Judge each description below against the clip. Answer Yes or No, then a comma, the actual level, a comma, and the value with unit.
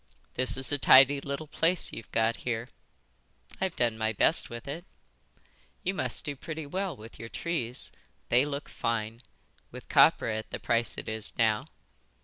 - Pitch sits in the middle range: No, low, 125 Hz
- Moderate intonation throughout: Yes, average, 4.5 semitones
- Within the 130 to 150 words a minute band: No, average, 165 wpm